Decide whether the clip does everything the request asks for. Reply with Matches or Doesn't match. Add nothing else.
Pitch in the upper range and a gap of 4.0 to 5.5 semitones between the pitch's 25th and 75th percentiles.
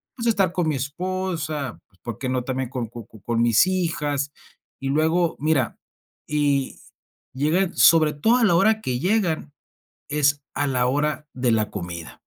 Doesn't match